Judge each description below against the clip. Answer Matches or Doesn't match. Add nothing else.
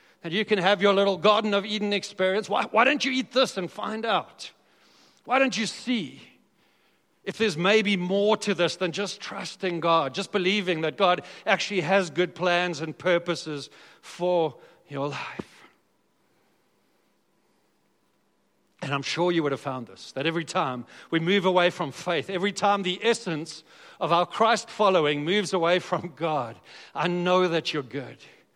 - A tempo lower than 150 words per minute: Doesn't match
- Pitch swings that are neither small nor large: Matches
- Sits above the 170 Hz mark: Matches